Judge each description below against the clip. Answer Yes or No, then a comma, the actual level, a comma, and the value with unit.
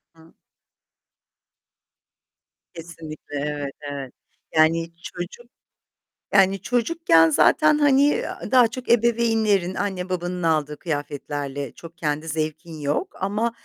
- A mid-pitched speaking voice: Yes, medium, 170 Hz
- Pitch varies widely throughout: Yes, wide, 6.3 semitones